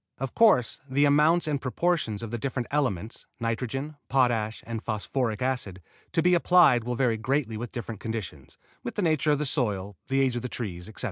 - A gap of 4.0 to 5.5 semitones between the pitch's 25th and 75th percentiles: Yes, average, 4.3 semitones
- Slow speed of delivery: No, average, 195 wpm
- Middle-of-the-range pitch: No, low, 125 Hz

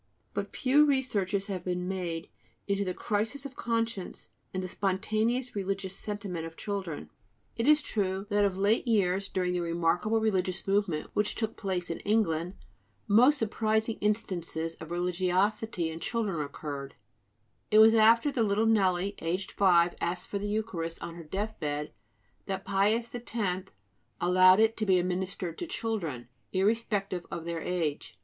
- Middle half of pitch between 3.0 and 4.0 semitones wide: Yes, average, 3.7 semitones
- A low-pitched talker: No, high, 195 Hz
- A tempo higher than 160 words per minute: No, average, 155 wpm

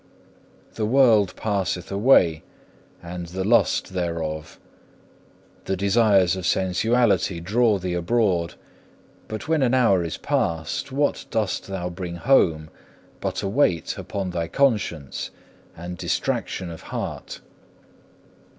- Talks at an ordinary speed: No, slow, 115 wpm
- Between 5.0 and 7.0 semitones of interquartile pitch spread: No, average, 4.5 semitones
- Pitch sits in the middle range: No, very low, 95 Hz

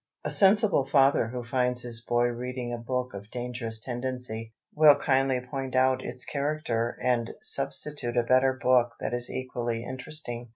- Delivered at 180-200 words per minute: No, average, 160 wpm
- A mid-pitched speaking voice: No, low, 125 Hz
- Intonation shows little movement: Yes, narrow, 1.6 semitones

